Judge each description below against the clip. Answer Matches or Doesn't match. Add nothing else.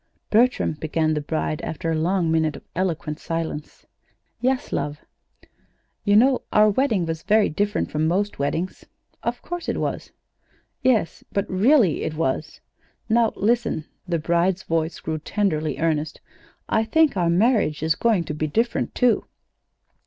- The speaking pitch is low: Doesn't match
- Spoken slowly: Doesn't match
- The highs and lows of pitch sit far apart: Matches